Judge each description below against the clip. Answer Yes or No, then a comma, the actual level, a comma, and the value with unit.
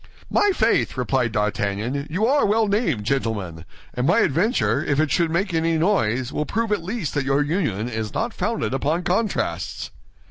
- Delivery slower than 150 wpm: No, average, 175 wpm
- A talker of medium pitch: Yes, medium, 155 Hz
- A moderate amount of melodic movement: No, wide, 8.7 semitones